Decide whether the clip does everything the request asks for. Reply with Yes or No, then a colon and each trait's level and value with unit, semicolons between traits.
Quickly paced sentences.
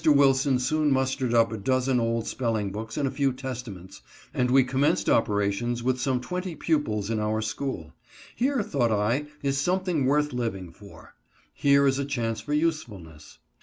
No: average, 165 wpm